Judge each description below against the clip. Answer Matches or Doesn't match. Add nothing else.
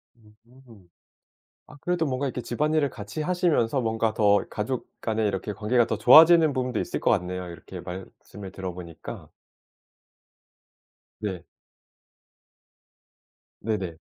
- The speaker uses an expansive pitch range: Doesn't match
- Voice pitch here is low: Matches